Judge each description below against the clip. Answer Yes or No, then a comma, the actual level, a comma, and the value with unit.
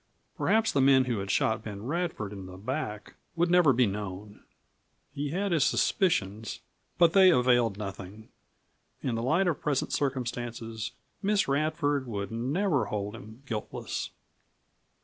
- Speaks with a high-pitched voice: No, low, 125 Hz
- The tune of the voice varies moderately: No, wide, 6.5 semitones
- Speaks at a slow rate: No, average, 145 wpm